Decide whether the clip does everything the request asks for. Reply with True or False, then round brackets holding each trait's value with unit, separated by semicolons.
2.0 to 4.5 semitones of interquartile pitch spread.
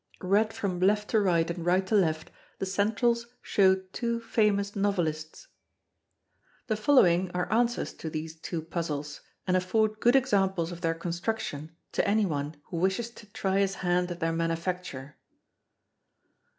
True (4.2 semitones)